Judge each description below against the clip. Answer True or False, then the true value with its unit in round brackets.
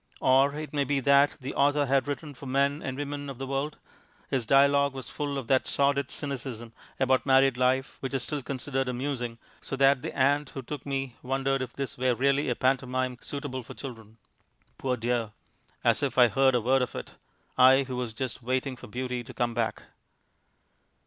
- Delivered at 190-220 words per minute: True (195 wpm)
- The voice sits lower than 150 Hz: True (135 Hz)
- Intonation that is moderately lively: False (1.7 semitones)